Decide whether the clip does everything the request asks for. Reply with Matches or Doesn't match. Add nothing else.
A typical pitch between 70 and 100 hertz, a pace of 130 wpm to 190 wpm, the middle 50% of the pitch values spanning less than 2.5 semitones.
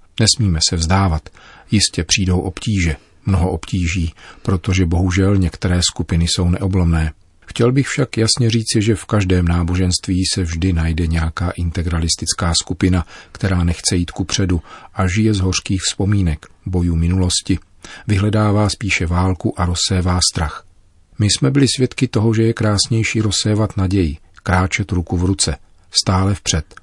Doesn't match